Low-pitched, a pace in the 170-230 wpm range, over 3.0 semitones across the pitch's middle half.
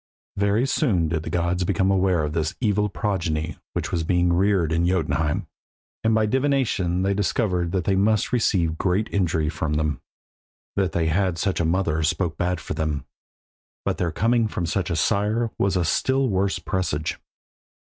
Yes: very low, 90 Hz; average, 175 wpm; average, 3.6 semitones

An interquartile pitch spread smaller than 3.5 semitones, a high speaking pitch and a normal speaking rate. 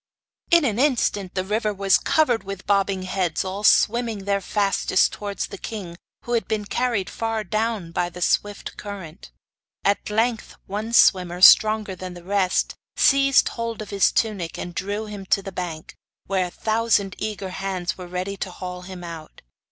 Yes: average, 2.9 semitones; high, 200 Hz; average, 175 wpm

